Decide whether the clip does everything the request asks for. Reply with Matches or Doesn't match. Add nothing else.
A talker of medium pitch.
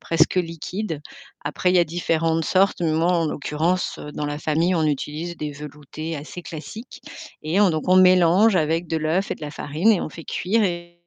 Matches